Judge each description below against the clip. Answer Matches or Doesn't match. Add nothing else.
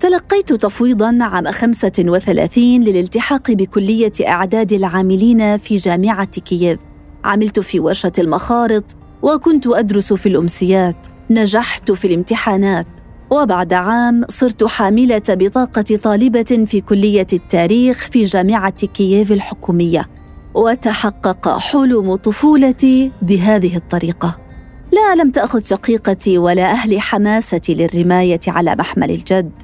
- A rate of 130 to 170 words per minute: Doesn't match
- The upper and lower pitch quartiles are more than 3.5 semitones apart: Matches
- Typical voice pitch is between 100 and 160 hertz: Doesn't match